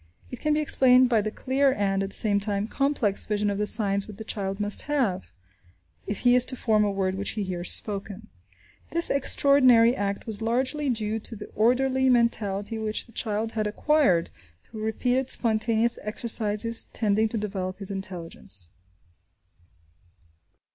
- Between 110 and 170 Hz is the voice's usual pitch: No, high, 215 Hz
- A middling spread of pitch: Yes, average, 3.5 semitones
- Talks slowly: No, average, 165 wpm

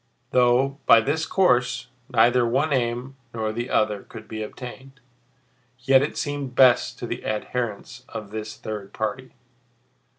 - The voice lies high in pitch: No, low, 125 Hz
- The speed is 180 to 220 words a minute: No, average, 140 wpm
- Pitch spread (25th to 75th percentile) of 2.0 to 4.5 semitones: Yes, average, 3.4 semitones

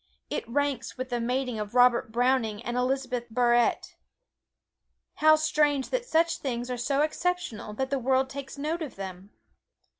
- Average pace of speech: Yes, average, 155 wpm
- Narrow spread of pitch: No, average, 3.3 semitones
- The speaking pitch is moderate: No, very high, 260 Hz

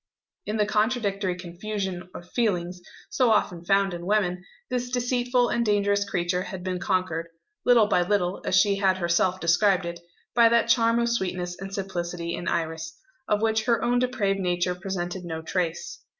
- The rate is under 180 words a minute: Yes, average, 170 wpm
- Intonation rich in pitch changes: No, average, 3.6 semitones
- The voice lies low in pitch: No, high, 190 Hz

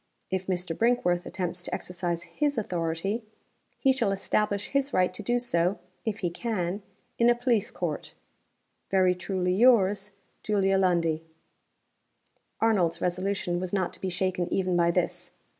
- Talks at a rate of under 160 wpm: Yes, average, 145 wpm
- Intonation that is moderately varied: Yes, average, 3.2 semitones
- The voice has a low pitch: No, high, 190 Hz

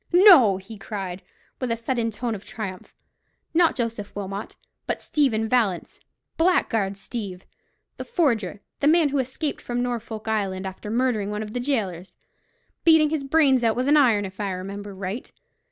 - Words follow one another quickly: No, average, 155 wpm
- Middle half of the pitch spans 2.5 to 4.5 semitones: No, average, 4.9 semitones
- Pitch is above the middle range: Yes, high, 225 Hz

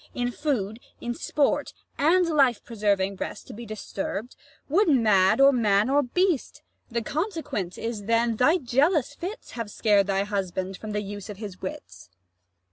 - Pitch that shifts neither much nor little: No, wide, 5.9 semitones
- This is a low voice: No, high, 230 Hz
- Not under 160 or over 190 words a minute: Yes, average, 165 wpm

